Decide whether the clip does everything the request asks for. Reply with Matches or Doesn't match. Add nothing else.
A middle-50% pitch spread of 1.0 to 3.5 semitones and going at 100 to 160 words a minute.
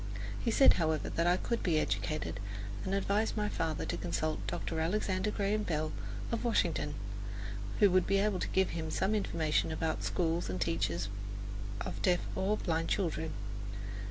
Doesn't match